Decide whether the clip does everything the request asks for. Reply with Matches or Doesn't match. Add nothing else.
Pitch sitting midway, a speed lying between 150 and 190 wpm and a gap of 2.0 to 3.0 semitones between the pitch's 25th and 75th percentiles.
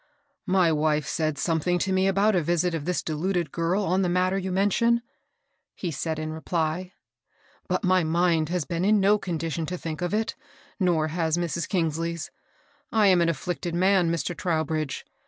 Matches